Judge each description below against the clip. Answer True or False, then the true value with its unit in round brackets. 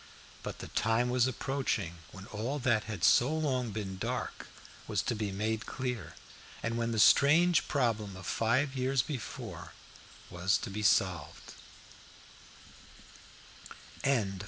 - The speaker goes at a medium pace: False (130 wpm)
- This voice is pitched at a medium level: False (115 Hz)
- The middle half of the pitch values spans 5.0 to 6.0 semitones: False (4.5 semitones)